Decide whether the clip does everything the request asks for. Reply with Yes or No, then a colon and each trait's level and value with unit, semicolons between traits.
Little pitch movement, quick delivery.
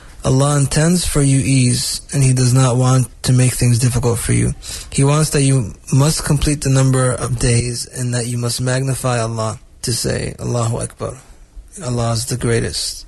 No: narrow, 2.3 semitones; average, 185 wpm